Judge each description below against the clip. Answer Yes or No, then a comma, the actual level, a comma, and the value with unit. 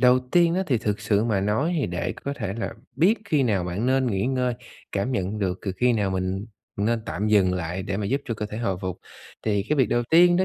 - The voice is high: No, low, 110 Hz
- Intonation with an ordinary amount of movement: Yes, average, 4.9 semitones